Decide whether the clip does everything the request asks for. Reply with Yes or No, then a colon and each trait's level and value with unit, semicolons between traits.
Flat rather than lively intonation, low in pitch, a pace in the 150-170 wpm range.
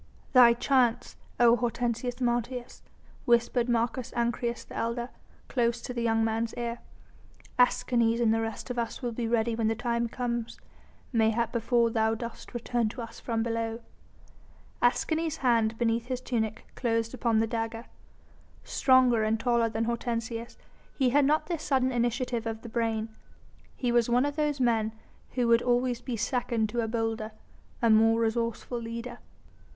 No: narrow, 1.3 semitones; high, 235 Hz; average, 160 wpm